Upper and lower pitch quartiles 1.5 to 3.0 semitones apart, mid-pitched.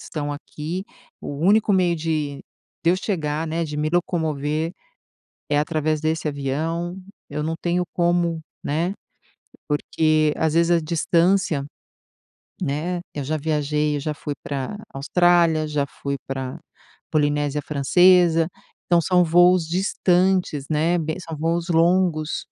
Yes: narrow, 2.6 semitones; medium, 160 Hz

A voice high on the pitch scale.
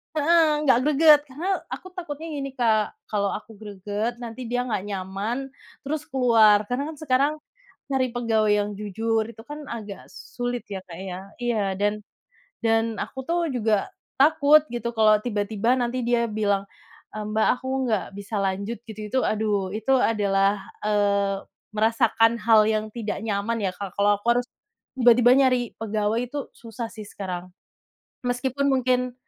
Yes: high, 225 Hz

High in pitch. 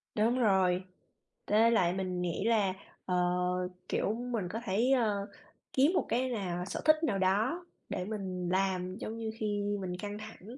Yes: high, 205 Hz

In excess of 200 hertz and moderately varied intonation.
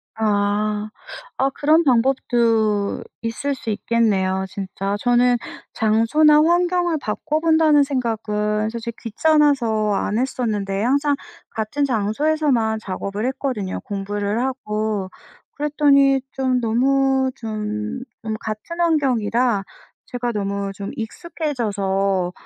Yes: high, 230 Hz; average, 4.5 semitones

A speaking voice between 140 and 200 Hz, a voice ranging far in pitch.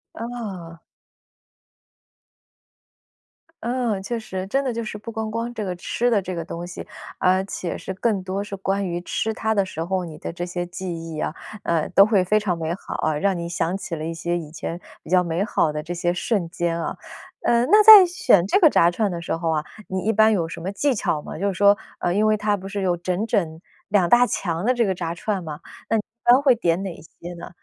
No: high, 190 Hz; average, 4.1 semitones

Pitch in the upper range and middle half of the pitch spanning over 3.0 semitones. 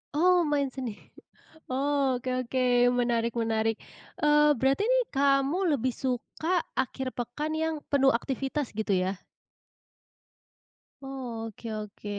Yes: very high, 265 Hz; average, 3.4 semitones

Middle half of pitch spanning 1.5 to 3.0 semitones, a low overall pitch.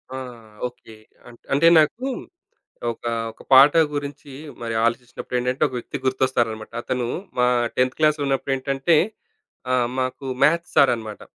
Yes: average, 2.7 semitones; low, 130 Hz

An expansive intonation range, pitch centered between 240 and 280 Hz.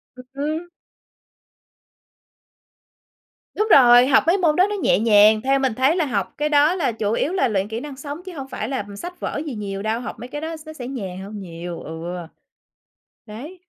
Yes: wide, 6.3 semitones; very high, 260 Hz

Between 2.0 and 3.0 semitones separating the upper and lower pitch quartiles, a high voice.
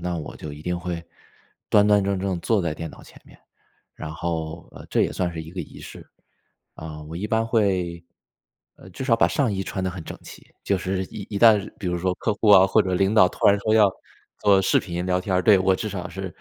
No: average, 2.7 semitones; very low, 95 Hz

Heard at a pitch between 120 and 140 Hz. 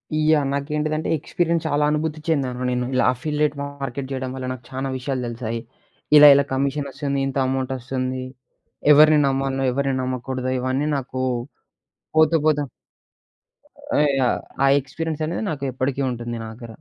Yes: low, 135 Hz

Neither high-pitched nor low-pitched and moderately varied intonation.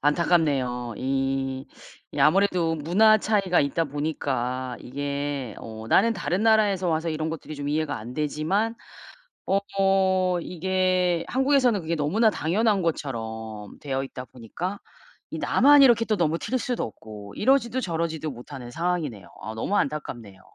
No: medium, 155 Hz; wide, 6.2 semitones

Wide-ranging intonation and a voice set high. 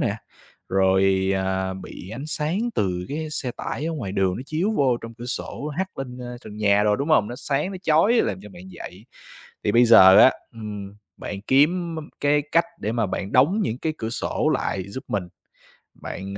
No: wide, 7.4 semitones; low, 120 Hz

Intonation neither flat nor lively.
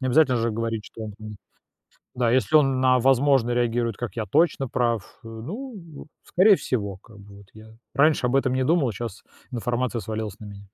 Yes: average, 3.5 semitones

